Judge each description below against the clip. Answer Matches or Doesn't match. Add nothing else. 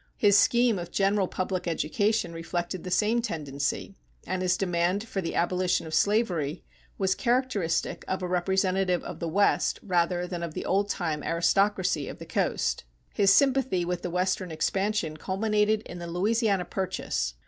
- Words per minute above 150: Matches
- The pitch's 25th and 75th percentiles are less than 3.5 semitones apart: Matches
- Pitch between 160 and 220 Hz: Matches